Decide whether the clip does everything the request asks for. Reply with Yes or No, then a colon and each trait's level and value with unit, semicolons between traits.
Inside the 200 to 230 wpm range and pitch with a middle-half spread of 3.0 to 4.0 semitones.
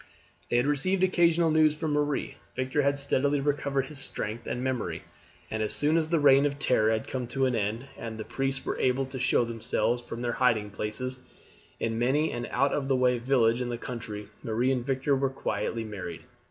Yes: fast, 205 wpm; average, 3.3 semitones